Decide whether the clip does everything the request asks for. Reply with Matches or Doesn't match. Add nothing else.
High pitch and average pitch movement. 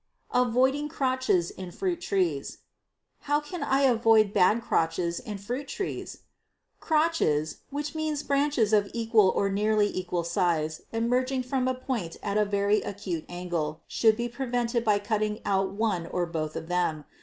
Doesn't match